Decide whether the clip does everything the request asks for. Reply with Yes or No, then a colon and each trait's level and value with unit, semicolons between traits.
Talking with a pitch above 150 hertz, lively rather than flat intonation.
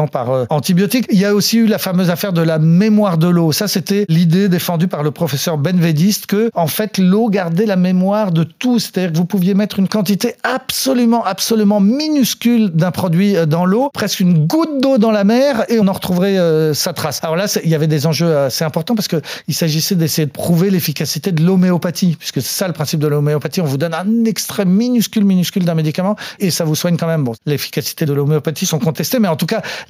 No: medium, 185 Hz; average, 4.4 semitones